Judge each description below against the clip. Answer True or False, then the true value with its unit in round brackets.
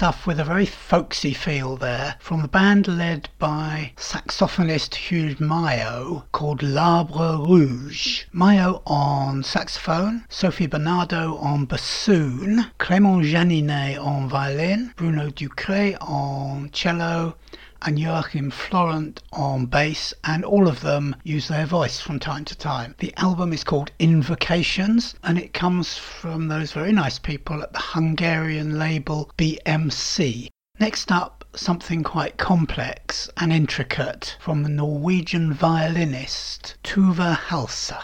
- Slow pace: True (125 wpm)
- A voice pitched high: False (160 Hz)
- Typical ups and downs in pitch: True (3.2 semitones)